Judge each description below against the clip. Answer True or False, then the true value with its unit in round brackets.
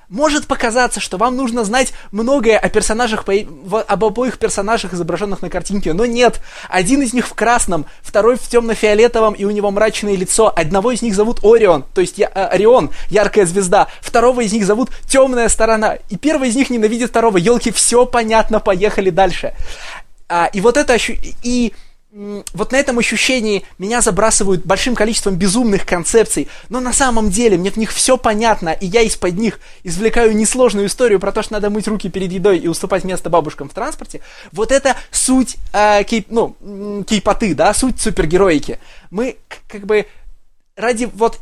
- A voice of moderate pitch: False (220 Hz)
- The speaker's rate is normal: False (170 wpm)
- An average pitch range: True (3.0 semitones)